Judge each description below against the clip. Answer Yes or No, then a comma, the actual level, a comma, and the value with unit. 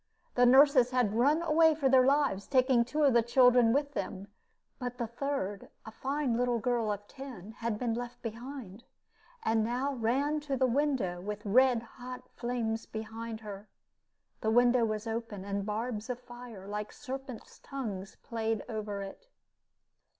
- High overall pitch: Yes, high, 240 Hz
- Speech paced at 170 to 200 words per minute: No, average, 160 wpm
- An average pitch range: Yes, average, 3.3 semitones